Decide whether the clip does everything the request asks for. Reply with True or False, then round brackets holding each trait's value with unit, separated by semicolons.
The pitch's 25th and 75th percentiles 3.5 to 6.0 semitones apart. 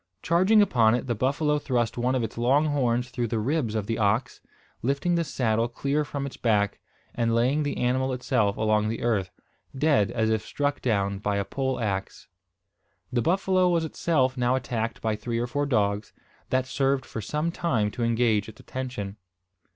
True (4.1 semitones)